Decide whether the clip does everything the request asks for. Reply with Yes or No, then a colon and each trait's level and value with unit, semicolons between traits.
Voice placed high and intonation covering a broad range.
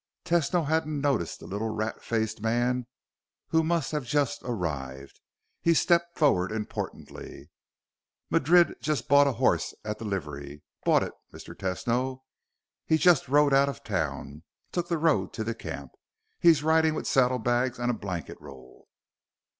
No: low, 125 Hz; wide, 6.4 semitones